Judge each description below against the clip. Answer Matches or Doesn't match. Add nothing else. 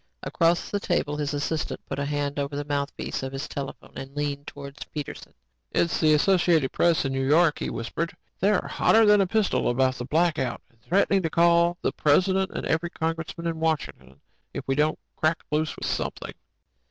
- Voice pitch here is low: Doesn't match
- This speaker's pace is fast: Doesn't match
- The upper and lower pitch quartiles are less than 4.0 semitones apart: Matches